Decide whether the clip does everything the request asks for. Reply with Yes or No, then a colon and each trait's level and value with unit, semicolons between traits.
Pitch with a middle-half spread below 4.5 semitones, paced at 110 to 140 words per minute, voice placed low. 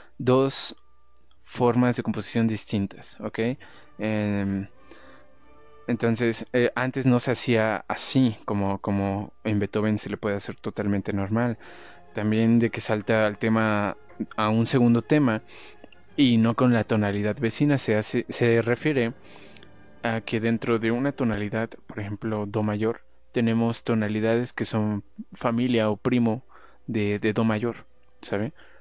Yes: narrow, 2.4 semitones; average, 135 wpm; low, 110 Hz